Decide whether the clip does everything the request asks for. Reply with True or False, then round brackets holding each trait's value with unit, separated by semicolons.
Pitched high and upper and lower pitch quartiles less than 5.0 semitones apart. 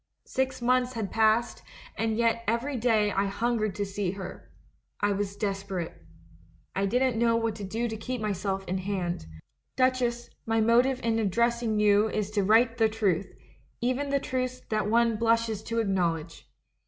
True (220 Hz; 2.9 semitones)